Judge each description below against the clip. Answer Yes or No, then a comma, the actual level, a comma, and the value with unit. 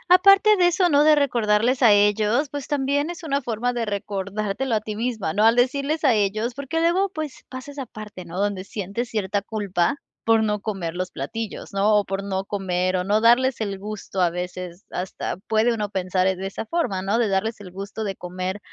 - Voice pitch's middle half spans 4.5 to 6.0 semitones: Yes, average, 4.8 semitones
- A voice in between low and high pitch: No, high, 215 Hz